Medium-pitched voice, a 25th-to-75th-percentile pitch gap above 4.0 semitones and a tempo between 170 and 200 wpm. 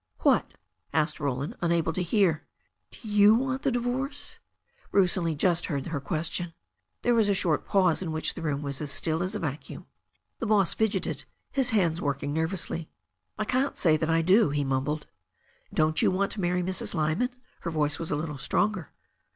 Yes: medium, 170 Hz; average, 4.8 semitones; average, 190 wpm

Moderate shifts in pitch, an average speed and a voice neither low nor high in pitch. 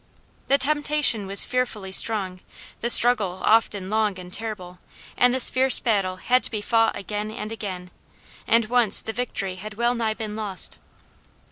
No: average, 3.6 semitones; average, 155 wpm; high, 215 Hz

